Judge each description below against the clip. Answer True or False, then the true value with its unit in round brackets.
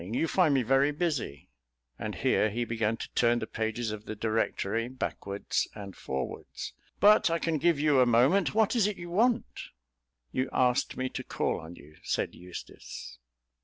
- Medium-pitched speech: False (125 Hz)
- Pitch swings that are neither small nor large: False (7.2 semitones)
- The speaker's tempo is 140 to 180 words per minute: True (175 wpm)